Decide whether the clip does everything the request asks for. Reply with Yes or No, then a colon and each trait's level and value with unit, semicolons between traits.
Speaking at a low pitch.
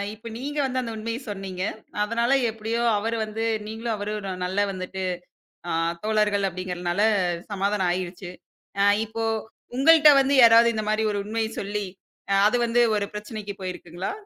No: high, 210 Hz